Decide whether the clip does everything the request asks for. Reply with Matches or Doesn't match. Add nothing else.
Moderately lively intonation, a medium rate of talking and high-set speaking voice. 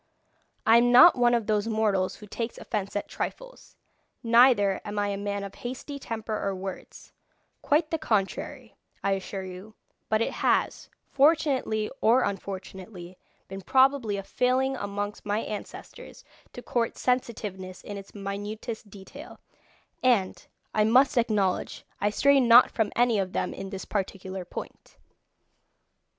Matches